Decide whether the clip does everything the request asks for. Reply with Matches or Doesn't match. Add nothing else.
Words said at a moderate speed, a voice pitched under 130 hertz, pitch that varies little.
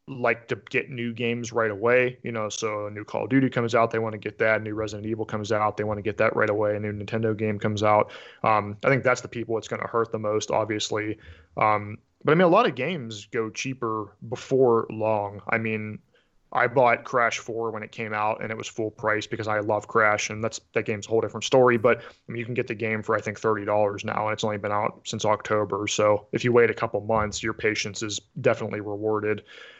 Doesn't match